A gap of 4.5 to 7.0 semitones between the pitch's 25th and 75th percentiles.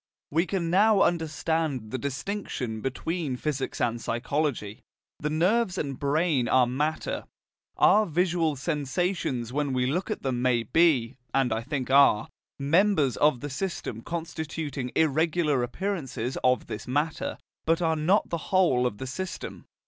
Yes: average, 4.9 semitones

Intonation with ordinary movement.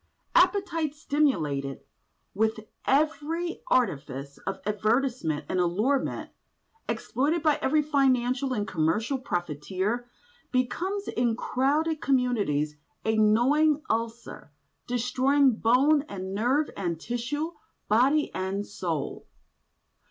No: wide, 6.5 semitones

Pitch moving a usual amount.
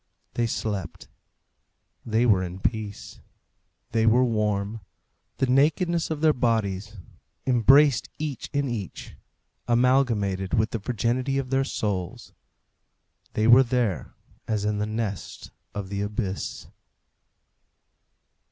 Yes: average, 3.9 semitones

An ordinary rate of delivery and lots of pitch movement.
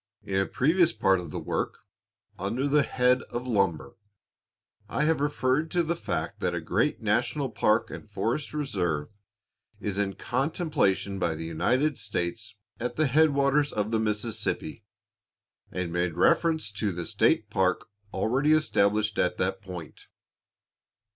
Yes: average, 145 wpm; wide, 6.7 semitones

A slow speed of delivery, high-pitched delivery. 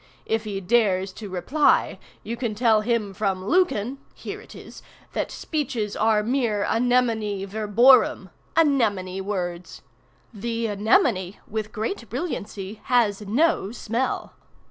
Yes: slow, 120 wpm; high, 220 Hz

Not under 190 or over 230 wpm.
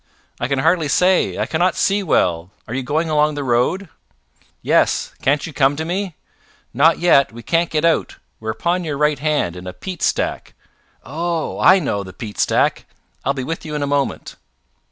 Yes: average, 195 wpm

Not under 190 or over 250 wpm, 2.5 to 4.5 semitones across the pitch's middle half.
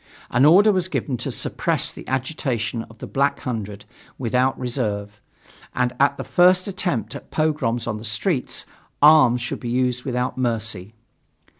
No: average, 155 wpm; average, 3.9 semitones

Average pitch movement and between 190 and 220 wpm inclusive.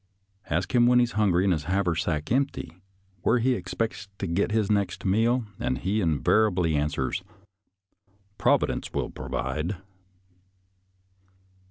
No: average, 4.1 semitones; slow, 135 wpm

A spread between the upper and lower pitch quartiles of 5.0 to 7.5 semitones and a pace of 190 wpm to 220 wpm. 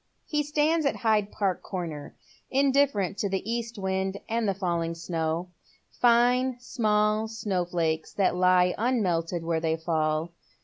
No: wide, 5.5 semitones; average, 145 wpm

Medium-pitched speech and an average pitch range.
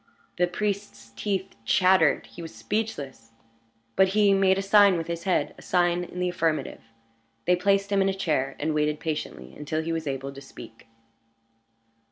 Yes: medium, 175 Hz; average, 4.4 semitones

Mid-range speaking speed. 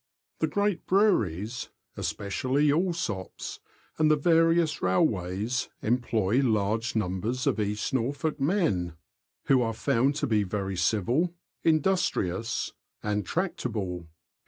No: slow, 110 wpm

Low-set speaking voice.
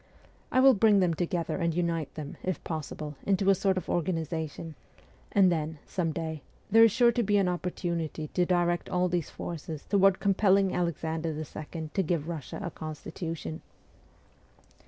No: medium, 170 Hz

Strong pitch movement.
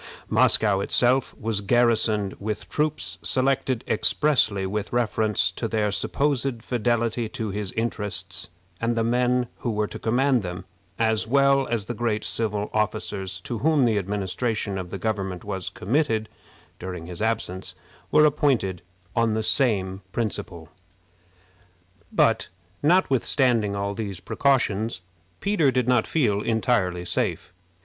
No: average, 3.6 semitones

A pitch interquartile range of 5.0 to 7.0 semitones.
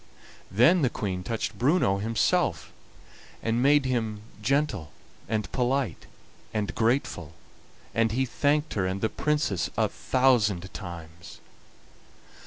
Yes: wide, 5.5 semitones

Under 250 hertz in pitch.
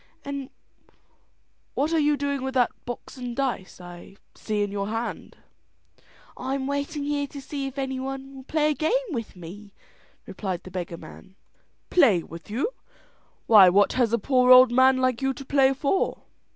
No: very high, 260 Hz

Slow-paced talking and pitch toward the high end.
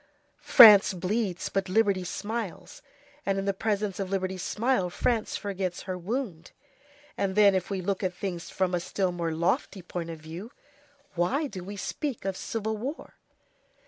No: average, 165 wpm; high, 195 Hz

